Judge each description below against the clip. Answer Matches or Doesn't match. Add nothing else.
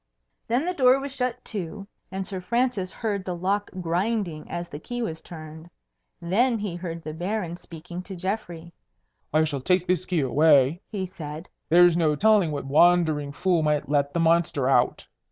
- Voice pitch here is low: Doesn't match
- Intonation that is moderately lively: Matches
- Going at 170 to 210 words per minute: Matches